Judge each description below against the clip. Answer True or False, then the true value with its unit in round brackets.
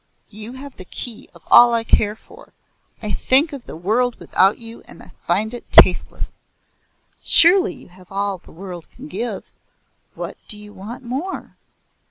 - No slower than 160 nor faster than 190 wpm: True (165 wpm)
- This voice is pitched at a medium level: False (220 Hz)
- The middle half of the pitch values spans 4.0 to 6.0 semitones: True (4.4 semitones)